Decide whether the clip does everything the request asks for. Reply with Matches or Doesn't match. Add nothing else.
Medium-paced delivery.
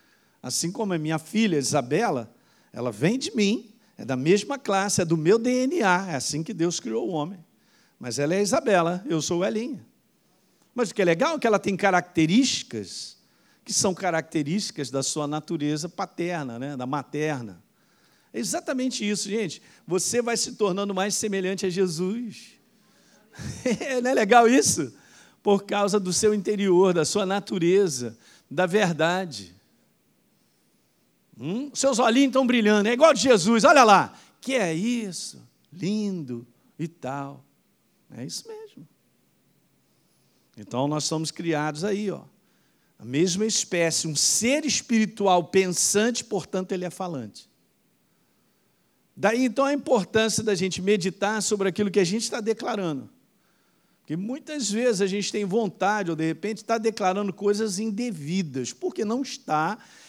Matches